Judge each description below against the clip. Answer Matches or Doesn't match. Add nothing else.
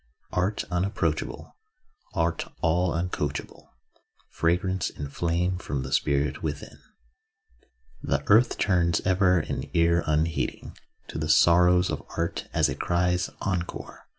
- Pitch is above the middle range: Doesn't match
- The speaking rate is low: Matches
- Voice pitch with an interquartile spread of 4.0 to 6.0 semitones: Doesn't match